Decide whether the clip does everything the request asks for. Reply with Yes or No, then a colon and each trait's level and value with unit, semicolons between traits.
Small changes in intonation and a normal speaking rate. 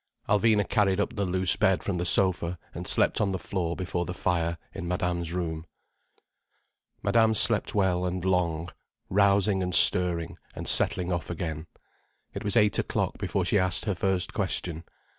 Yes: narrow, 2.3 semitones; average, 165 wpm